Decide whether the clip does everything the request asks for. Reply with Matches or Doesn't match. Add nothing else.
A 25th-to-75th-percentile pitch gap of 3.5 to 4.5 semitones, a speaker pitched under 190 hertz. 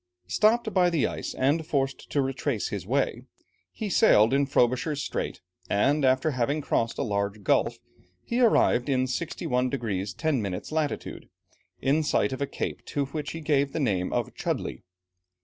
Matches